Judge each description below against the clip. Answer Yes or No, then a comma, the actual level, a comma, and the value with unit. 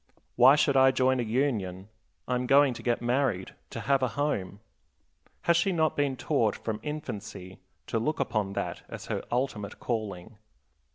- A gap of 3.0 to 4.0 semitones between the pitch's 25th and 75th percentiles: No, average, 4.7 semitones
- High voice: No, low, 125 Hz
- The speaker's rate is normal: Yes, average, 170 wpm